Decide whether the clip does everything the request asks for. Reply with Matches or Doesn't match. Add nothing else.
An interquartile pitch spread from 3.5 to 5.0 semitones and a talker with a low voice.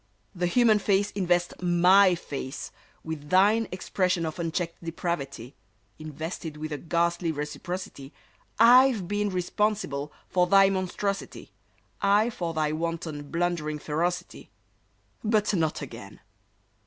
Doesn't match